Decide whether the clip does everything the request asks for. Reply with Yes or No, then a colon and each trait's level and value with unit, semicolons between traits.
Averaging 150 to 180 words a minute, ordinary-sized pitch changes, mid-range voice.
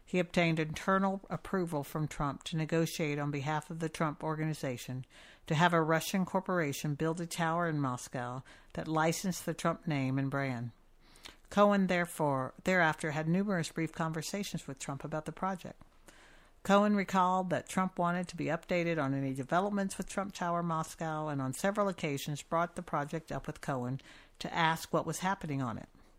Yes: average, 170 wpm; average, 3.5 semitones; medium, 160 Hz